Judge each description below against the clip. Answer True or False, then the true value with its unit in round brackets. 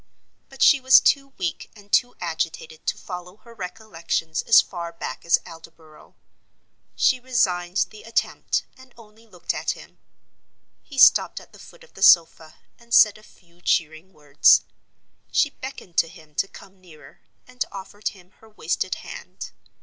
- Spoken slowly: False (160 wpm)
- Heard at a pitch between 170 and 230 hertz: True (190 Hz)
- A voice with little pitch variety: False (5.5 semitones)